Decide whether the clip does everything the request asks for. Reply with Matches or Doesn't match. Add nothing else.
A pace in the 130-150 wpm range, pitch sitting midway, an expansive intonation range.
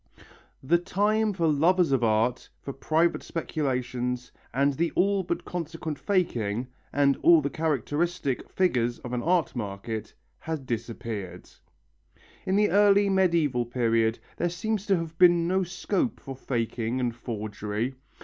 Matches